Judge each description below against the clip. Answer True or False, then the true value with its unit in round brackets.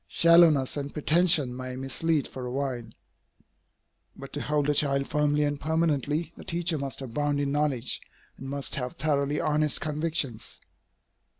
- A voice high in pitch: False (145 Hz)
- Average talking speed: True (145 wpm)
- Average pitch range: False (2.2 semitones)